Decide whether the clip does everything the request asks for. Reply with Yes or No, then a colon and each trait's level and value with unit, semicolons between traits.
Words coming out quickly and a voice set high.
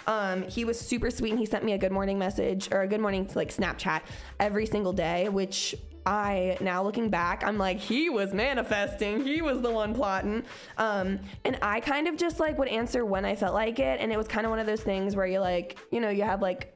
Yes: fast, 245 wpm; high, 205 Hz